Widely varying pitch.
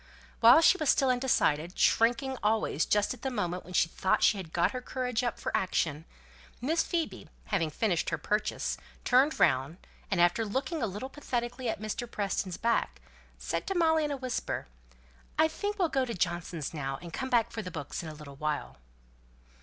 Yes: wide, 7.2 semitones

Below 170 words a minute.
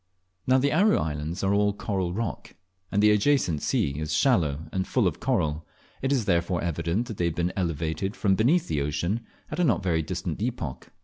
No: average, 200 wpm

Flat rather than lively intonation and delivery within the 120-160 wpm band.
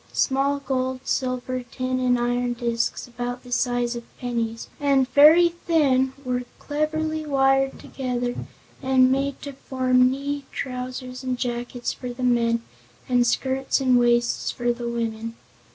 Yes: narrow, 1.8 semitones; average, 140 wpm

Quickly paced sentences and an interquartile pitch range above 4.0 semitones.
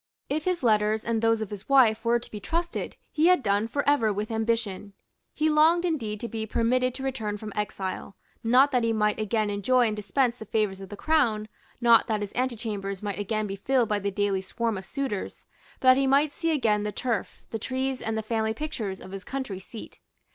No: fast, 220 wpm; average, 3.7 semitones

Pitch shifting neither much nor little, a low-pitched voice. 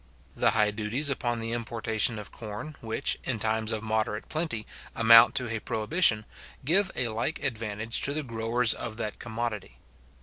No: narrow, 1.9 semitones; low, 115 Hz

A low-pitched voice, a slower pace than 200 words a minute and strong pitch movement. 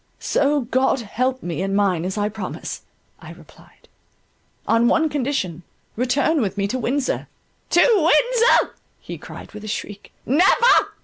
No: high, 245 Hz; average, 145 wpm; wide, 5.9 semitones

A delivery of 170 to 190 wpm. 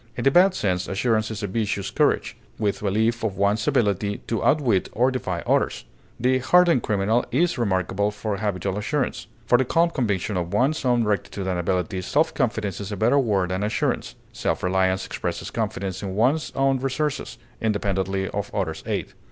Yes: average, 175 wpm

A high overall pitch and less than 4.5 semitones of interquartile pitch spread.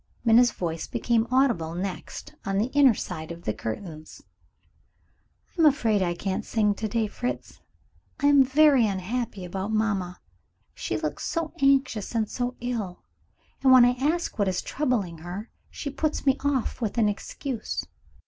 No: high, 225 Hz; wide, 5.4 semitones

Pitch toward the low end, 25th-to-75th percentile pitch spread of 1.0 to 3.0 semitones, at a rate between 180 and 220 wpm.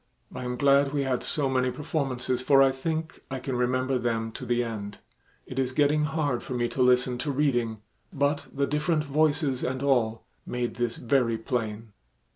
Yes: low, 130 Hz; average, 2.7 semitones; average, 185 wpm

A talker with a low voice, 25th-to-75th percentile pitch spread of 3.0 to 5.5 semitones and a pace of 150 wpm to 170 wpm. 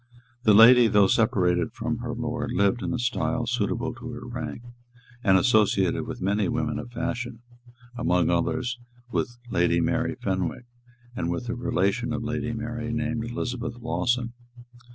Yes: low, 115 Hz; average, 3.3 semitones; average, 155 wpm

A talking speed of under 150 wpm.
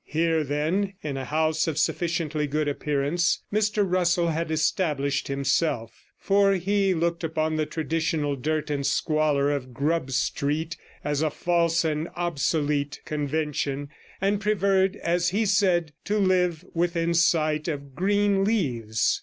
Yes: slow, 135 wpm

